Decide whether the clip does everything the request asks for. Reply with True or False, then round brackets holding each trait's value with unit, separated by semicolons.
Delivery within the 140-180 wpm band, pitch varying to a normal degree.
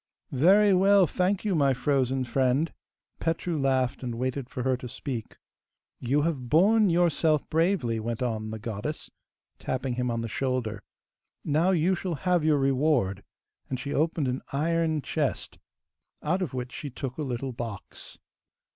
True (155 wpm; 4.8 semitones)